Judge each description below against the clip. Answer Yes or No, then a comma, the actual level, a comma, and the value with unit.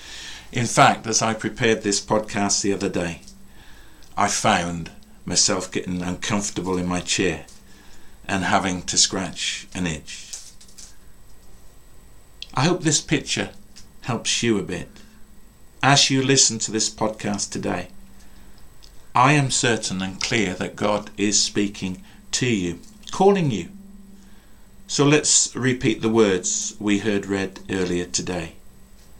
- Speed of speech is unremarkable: No, slow, 125 wpm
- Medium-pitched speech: No, low, 105 Hz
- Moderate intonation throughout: Yes, average, 4.2 semitones